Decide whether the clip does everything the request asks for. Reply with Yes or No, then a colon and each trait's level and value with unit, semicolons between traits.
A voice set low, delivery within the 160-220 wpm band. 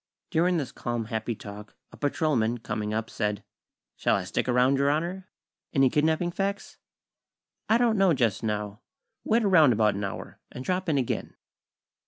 Yes: low, 130 Hz; average, 165 wpm